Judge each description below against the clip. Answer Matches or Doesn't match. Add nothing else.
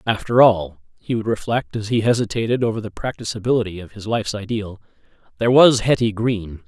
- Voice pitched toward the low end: Matches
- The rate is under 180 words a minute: Matches